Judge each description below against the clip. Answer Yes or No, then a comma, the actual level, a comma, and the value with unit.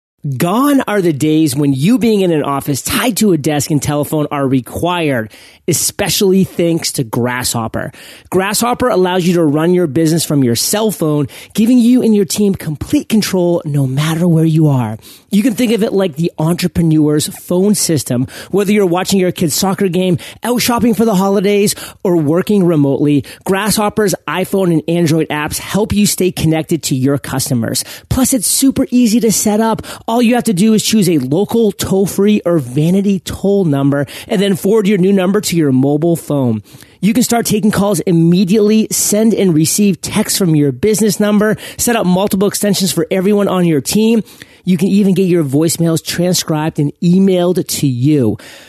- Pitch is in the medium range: Yes, medium, 180 Hz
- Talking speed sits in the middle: Yes, average, 180 wpm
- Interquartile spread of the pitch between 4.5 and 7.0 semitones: Yes, average, 5.1 semitones